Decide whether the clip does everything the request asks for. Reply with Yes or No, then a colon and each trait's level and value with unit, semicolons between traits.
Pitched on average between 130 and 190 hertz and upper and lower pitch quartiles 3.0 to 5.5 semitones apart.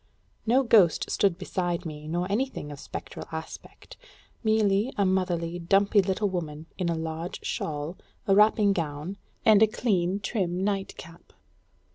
Yes: medium, 185 Hz; average, 3.4 semitones